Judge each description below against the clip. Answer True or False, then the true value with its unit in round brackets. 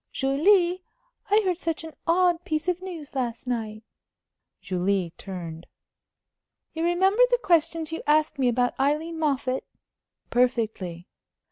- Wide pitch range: True (6.3 semitones)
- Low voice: False (300 Hz)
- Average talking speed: False (125 wpm)